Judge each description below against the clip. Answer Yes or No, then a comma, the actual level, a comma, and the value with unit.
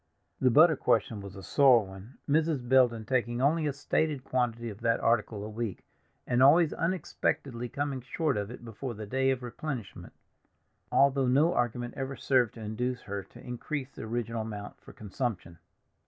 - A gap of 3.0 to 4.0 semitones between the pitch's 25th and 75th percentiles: Yes, average, 3.6 semitones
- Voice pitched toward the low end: Yes, low, 125 Hz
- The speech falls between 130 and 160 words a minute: No, average, 170 wpm